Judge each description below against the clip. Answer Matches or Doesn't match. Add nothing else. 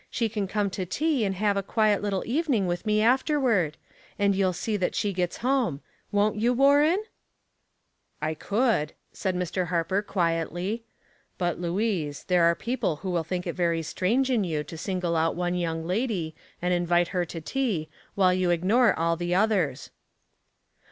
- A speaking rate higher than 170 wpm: Matches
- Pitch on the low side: Doesn't match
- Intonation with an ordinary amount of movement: Matches